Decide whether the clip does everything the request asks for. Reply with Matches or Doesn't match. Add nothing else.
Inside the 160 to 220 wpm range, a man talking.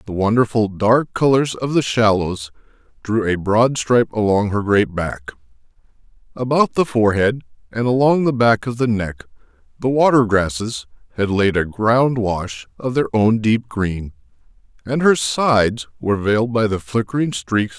Matches